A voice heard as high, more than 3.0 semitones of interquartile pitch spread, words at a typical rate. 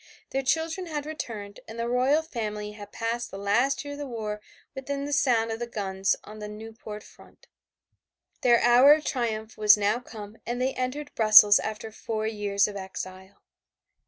Yes: high, 225 Hz; average, 3.7 semitones; average, 175 wpm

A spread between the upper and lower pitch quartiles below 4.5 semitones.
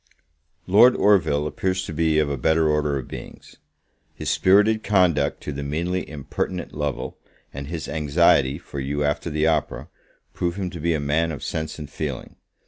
Yes: average, 3.2 semitones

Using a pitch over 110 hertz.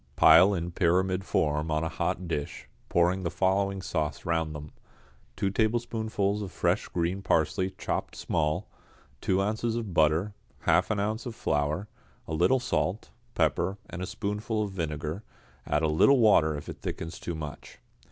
No: very low, 90 Hz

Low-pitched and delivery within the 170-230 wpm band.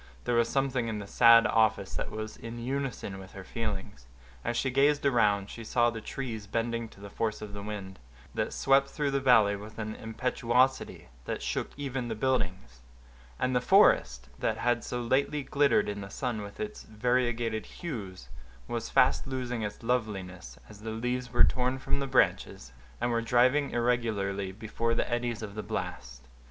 Yes: low, 115 Hz; average, 180 wpm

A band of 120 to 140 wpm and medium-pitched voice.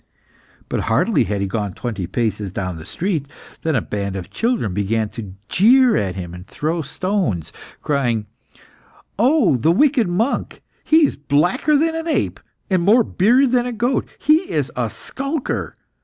No: average, 165 wpm; medium, 165 Hz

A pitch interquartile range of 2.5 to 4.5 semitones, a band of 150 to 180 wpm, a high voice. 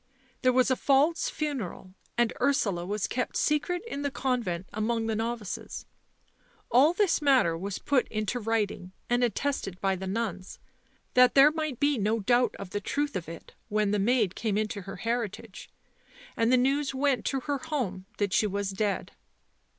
No: average, 5.2 semitones; average, 175 wpm; high, 230 Hz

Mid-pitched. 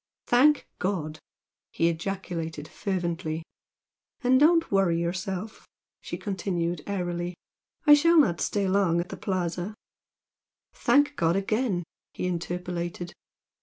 Yes: medium, 180 Hz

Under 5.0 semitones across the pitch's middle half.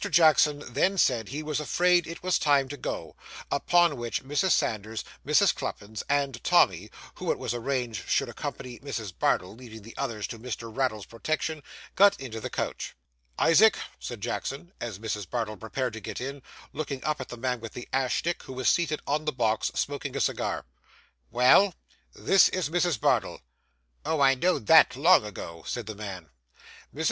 No: wide, 5.4 semitones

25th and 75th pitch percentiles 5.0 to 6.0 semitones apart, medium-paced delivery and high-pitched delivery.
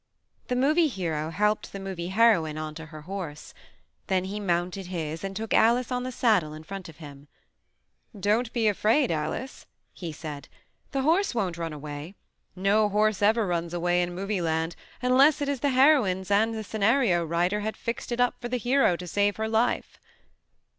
Yes: wide, 5.4 semitones; average, 180 wpm; high, 195 Hz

